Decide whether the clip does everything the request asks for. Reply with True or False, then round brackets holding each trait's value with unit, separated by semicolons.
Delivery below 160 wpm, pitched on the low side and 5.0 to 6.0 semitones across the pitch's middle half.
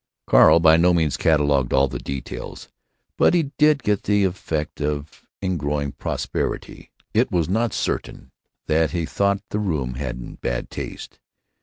True (150 wpm; 80 Hz; 5.3 semitones)